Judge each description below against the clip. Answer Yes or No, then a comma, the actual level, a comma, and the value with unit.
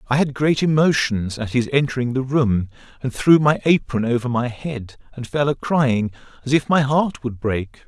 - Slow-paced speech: No, average, 200 wpm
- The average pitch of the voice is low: Yes, low, 130 Hz